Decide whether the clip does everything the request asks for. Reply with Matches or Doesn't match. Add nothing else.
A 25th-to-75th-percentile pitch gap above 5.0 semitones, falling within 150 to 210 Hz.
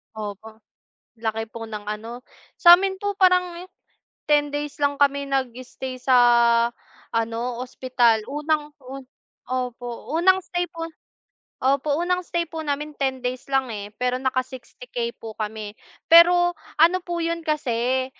Doesn't match